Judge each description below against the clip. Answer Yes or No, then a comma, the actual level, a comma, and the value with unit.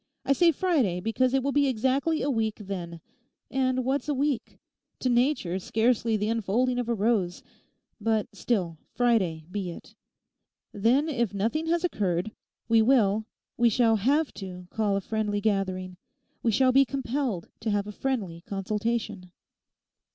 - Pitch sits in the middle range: No, high, 225 Hz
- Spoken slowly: No, average, 150 wpm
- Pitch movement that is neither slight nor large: Yes, average, 4.6 semitones